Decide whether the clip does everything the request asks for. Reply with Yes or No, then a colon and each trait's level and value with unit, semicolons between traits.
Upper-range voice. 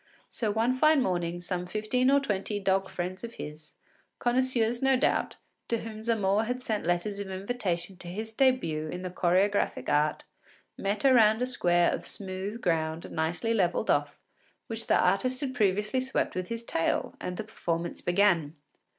Yes: high, 200 Hz